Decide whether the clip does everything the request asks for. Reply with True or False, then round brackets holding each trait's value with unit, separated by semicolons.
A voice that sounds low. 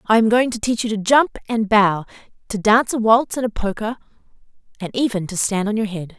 False (215 Hz)